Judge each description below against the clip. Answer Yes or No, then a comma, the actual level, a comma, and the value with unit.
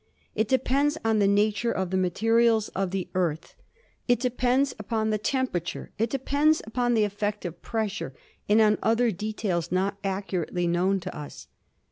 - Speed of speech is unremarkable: Yes, average, 160 wpm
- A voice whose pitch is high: Yes, high, 210 Hz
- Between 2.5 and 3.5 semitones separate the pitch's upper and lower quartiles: No, average, 3.9 semitones